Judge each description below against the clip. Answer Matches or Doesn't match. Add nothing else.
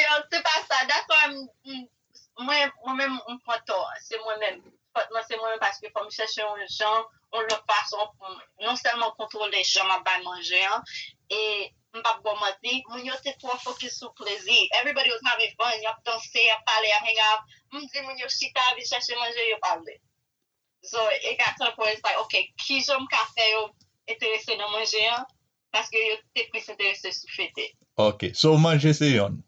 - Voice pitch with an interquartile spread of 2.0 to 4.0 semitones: Matches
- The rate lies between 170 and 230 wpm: Matches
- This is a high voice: Matches